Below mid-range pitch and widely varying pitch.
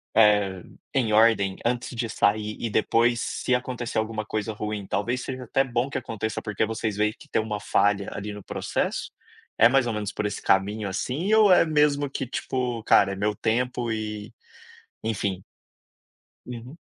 No: low, 110 Hz; average, 3.0 semitones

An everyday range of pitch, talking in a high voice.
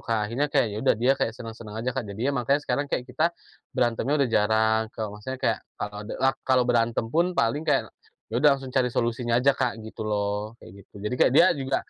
No: average, 3.5 semitones; low, 120 Hz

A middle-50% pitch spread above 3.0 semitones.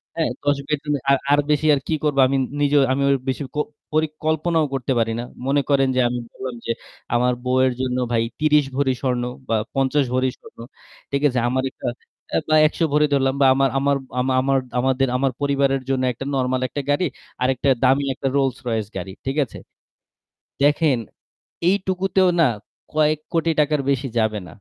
No: narrow, 2.4 semitones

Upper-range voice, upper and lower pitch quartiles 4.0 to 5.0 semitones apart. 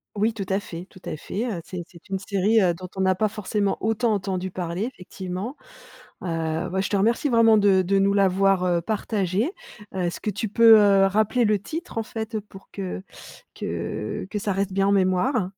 No: high, 195 Hz; average, 2.7 semitones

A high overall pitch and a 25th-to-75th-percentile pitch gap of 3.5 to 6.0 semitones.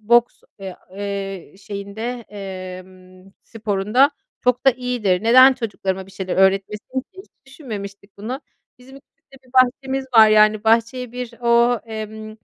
Yes: high, 220 Hz; average, 4.0 semitones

